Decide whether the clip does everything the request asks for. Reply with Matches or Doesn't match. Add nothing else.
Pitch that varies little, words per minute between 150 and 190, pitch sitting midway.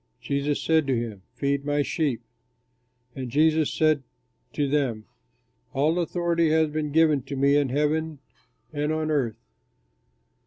Doesn't match